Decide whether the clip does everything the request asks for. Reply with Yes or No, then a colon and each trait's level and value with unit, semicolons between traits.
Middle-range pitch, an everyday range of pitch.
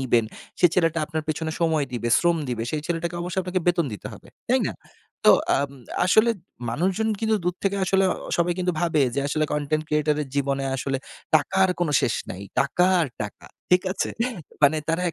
Yes: medium, 160 Hz; average, 4.0 semitones